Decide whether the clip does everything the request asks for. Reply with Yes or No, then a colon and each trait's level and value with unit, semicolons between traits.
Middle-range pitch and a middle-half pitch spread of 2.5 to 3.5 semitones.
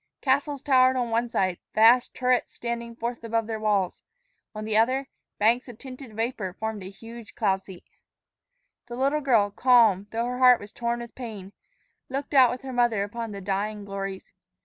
No: high, 230 Hz; average, 3.2 semitones